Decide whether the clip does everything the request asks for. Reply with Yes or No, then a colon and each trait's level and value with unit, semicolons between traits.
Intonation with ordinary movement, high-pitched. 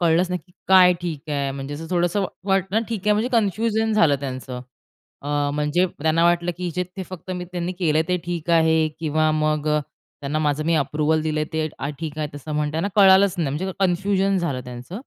No: average, 3.5 semitones; medium, 165 Hz